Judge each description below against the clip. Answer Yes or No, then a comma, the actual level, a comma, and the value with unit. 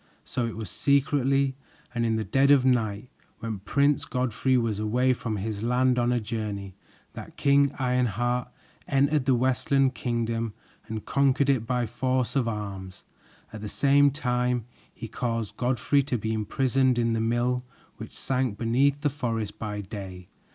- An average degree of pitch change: Yes, average, 3.1 semitones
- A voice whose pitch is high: No, low, 125 Hz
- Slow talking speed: No, average, 160 wpm